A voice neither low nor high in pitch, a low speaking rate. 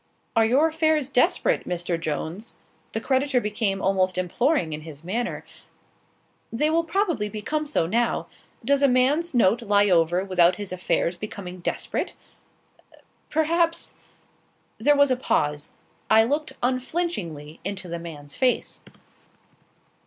No: high, 220 Hz; slow, 130 wpm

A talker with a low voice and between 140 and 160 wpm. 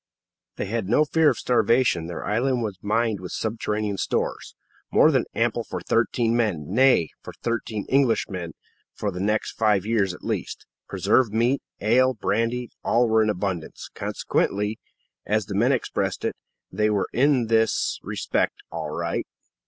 Yes: low, 110 Hz; average, 155 wpm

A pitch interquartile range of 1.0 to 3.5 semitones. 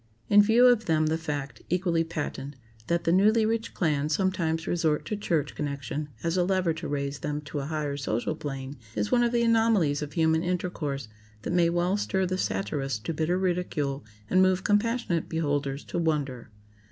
No: average, 4.4 semitones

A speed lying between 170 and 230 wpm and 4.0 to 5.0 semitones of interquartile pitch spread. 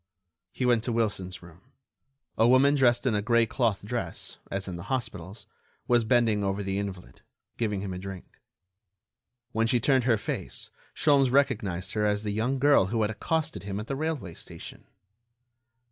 Yes: average, 175 wpm; average, 4.3 semitones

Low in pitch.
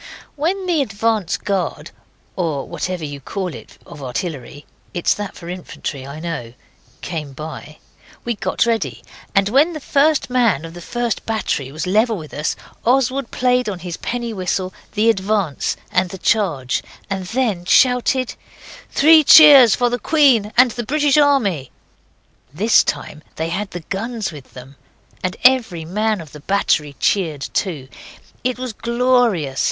No: high, 200 Hz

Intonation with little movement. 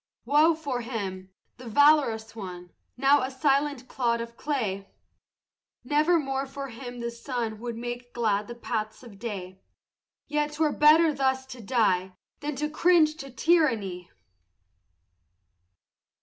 No: average, 4.7 semitones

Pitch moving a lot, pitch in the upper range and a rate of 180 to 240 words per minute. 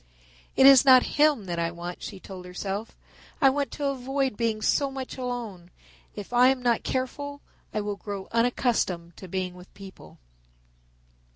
No: wide, 5.8 semitones; high, 230 Hz; average, 165 wpm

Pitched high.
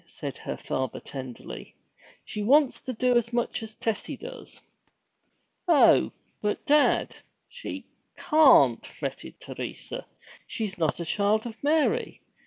Yes: high, 230 Hz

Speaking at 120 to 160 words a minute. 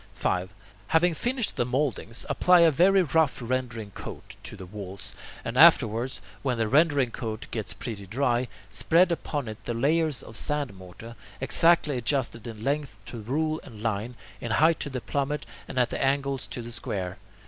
No: average, 175 wpm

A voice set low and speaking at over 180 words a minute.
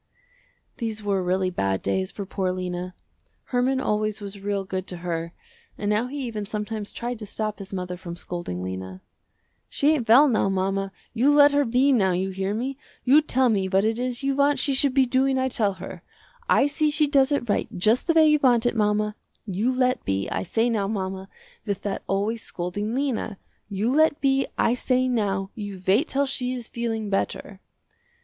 No: high, 215 Hz; average, 200 wpm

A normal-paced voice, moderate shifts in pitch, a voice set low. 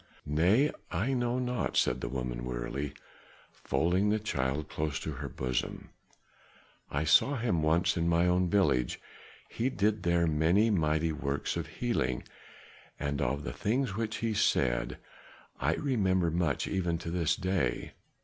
No: average, 150 wpm; wide, 6.3 semitones; very low, 85 Hz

